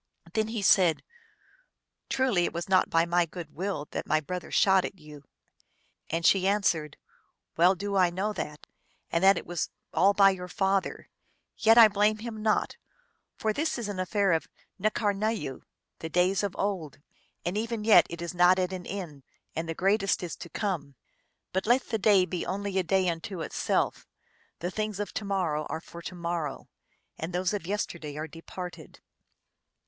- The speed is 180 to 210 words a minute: Yes, average, 185 wpm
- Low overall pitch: No, medium, 185 Hz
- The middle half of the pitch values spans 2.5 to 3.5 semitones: Yes, average, 3.2 semitones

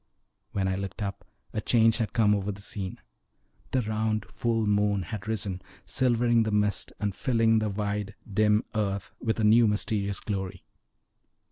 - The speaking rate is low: No, average, 160 wpm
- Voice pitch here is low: Yes, low, 105 Hz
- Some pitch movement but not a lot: No, narrow, 1.9 semitones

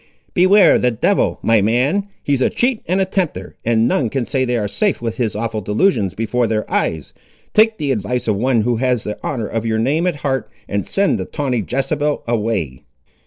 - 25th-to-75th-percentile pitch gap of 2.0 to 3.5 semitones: No, average, 5.2 semitones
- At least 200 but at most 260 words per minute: Yes, fast, 205 wpm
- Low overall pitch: Yes, low, 125 Hz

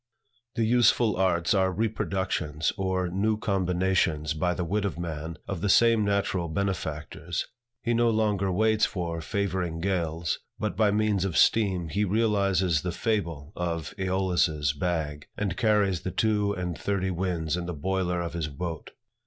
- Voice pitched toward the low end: Yes, very low, 95 Hz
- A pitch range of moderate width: Yes, average, 3.3 semitones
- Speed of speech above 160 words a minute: No, average, 155 wpm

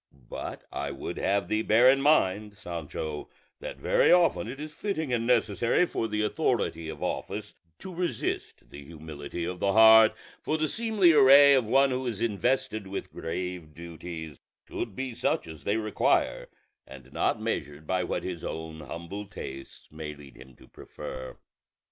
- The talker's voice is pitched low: Yes, low, 100 Hz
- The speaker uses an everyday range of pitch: No, wide, 8.2 semitones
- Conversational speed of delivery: Yes, average, 165 wpm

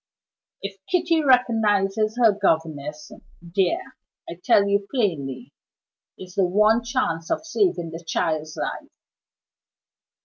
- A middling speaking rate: No, slow, 110 wpm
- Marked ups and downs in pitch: Yes, wide, 6.0 semitones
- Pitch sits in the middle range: No, high, 200 Hz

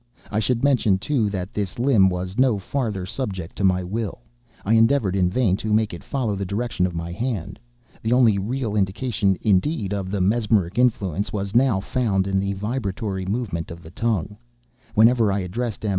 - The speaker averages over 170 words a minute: Yes, average, 190 wpm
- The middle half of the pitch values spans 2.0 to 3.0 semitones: No, average, 3.7 semitones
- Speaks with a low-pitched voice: Yes, low, 105 Hz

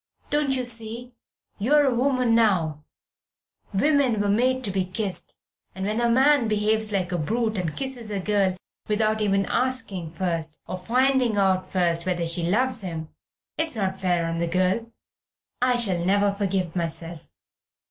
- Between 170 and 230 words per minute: No, average, 160 wpm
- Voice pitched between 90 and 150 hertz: No, high, 205 Hz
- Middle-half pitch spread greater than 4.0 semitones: Yes, average, 4.8 semitones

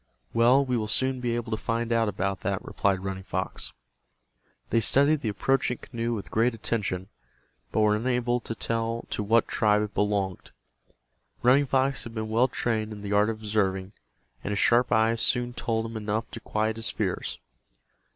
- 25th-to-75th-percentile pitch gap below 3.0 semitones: Yes, narrow, 2.4 semitones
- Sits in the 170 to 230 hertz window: No, low, 110 Hz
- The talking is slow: No, average, 180 wpm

